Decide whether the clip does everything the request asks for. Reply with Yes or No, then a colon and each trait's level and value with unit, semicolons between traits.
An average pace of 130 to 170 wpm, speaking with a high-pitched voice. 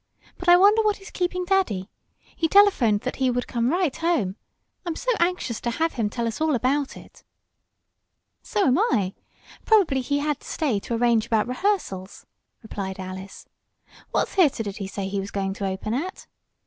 No: average, 185 wpm; very high, 255 Hz